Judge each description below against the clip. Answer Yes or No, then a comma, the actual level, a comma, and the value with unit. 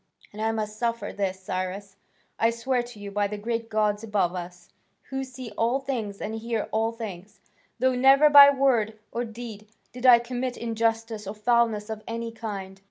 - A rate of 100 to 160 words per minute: No, average, 180 wpm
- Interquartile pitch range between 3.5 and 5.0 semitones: No, narrow, 2.5 semitones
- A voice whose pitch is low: No, high, 225 Hz